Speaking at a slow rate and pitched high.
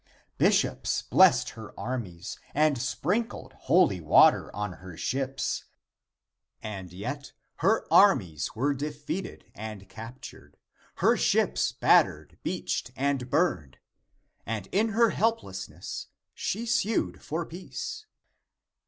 No: slow, 105 wpm; low, 135 Hz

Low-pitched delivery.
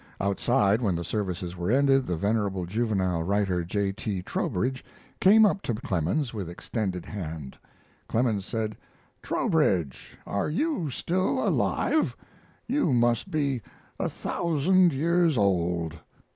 Yes: low, 105 Hz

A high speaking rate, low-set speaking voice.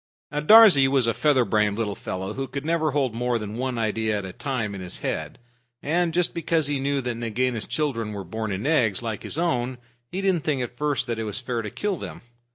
Yes: fast, 230 wpm; low, 125 Hz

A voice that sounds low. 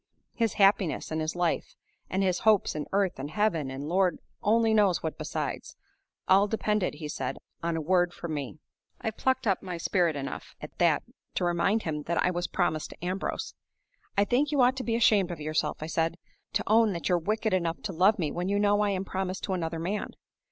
No: medium, 185 Hz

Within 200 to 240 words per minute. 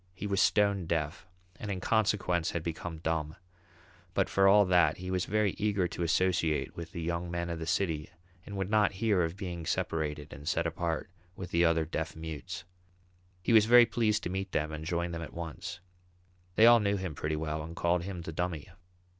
Yes: fast, 205 wpm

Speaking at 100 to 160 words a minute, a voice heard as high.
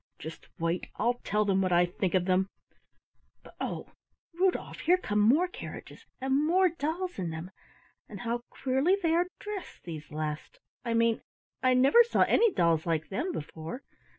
No: average, 170 wpm; high, 230 Hz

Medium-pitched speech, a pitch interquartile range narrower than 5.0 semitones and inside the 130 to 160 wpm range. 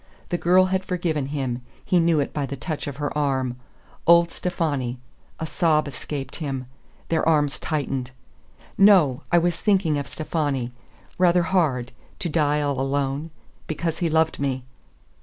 Yes: medium, 150 Hz; average, 3.6 semitones; average, 155 wpm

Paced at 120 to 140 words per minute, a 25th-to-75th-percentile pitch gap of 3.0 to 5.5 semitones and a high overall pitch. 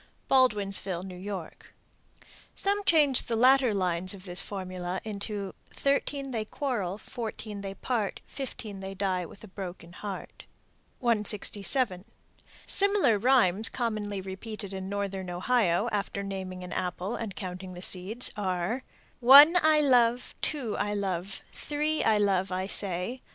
Yes: slow, 135 wpm; average, 4.4 semitones; high, 200 Hz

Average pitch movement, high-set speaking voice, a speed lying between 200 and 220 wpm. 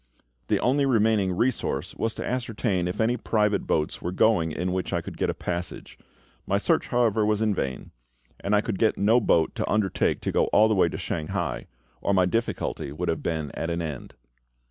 No: average, 4.4 semitones; low, 100 Hz; fast, 205 wpm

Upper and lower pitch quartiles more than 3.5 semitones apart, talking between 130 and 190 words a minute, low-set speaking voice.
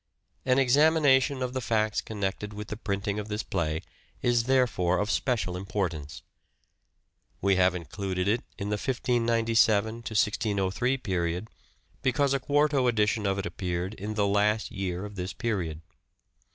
Yes: average, 4.1 semitones; average, 145 wpm; low, 105 Hz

